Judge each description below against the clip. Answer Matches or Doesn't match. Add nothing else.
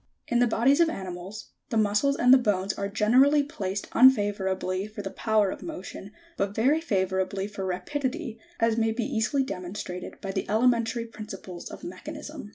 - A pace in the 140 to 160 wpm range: Doesn't match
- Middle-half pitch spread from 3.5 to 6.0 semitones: Matches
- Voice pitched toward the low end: Doesn't match